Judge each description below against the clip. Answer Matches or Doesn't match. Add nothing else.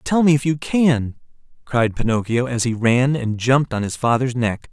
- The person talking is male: Matches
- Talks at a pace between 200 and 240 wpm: Matches